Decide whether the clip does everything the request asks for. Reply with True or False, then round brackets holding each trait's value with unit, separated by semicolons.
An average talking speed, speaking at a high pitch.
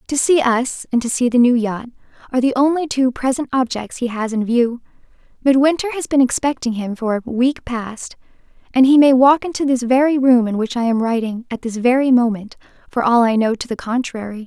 False (215 wpm; 250 Hz)